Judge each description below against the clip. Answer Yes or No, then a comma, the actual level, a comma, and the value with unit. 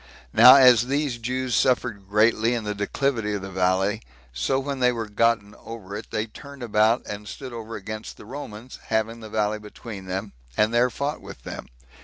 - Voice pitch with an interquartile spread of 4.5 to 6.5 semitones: No, average, 3.0 semitones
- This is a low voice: Yes, low, 110 Hz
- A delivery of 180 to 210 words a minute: Yes, average, 190 wpm